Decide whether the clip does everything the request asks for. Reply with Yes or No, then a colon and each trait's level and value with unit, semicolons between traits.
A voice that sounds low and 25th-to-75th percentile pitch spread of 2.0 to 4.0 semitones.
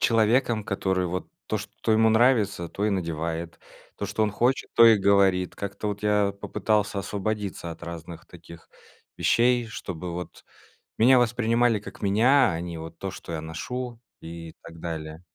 No: low, 100 Hz; average, 4.7 semitones